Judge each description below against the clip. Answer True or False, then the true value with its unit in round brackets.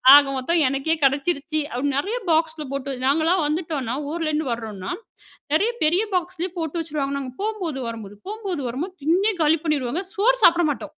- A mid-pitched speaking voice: False (310 Hz)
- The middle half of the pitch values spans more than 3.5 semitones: True (4.1 semitones)